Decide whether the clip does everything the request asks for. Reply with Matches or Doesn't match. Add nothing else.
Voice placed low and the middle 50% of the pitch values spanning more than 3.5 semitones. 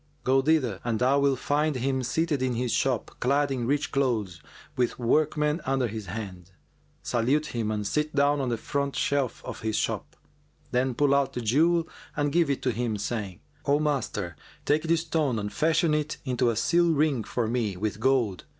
Matches